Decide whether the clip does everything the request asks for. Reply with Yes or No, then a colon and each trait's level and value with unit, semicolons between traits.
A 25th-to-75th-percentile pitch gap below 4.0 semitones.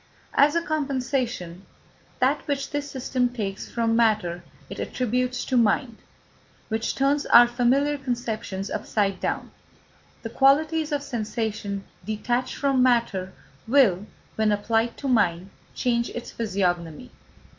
No: average, 4.3 semitones